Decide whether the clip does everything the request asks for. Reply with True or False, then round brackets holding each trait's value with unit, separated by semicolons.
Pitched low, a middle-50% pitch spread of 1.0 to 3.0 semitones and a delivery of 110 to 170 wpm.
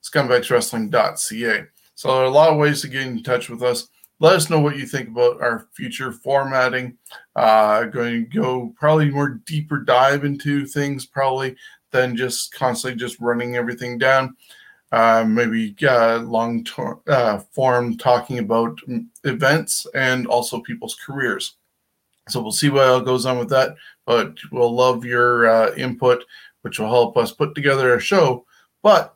True (125 Hz; 2.4 semitones; 165 wpm)